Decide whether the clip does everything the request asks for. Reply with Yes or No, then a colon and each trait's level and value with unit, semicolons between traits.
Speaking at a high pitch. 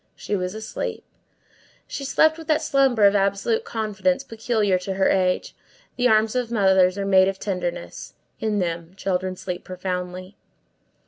Yes: high, 195 Hz